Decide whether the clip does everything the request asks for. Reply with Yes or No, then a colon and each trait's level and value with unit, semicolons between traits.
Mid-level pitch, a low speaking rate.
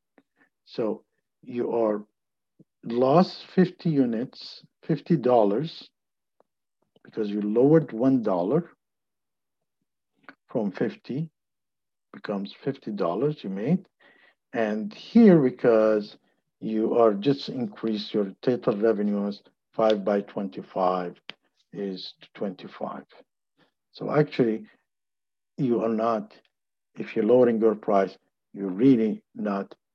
No: low, 110 Hz; slow, 95 wpm